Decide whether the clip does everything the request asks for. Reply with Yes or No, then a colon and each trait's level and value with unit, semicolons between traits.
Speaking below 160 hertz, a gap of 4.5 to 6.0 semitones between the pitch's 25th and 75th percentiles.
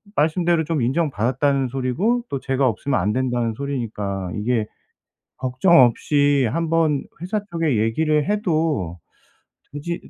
Yes: medium, 140 Hz; average, 5.1 semitones